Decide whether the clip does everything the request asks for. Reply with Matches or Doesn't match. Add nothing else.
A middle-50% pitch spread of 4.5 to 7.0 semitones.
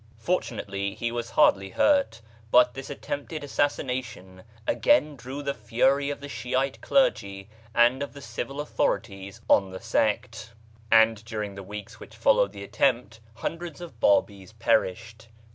Matches